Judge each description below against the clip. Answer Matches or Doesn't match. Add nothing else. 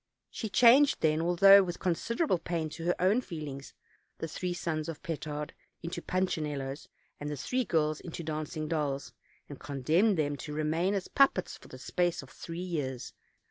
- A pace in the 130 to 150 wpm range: Doesn't match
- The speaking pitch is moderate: Matches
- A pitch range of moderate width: Matches